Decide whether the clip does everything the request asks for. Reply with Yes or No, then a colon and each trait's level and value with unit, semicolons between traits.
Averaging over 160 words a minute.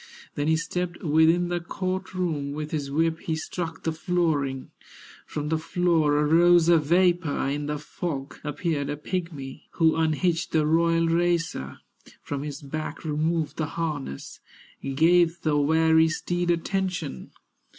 No: average, 140 wpm